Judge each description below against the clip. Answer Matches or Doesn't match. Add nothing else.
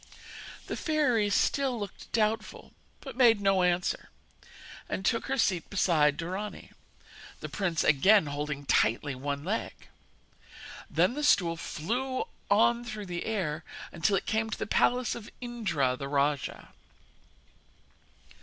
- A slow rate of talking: Matches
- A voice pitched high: Matches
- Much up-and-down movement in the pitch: Matches